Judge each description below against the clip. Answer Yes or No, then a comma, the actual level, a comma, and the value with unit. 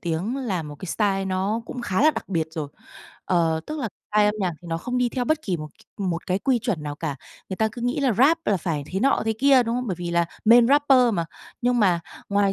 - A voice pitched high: Yes, high, 205 Hz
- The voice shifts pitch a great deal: Yes, wide, 6.2 semitones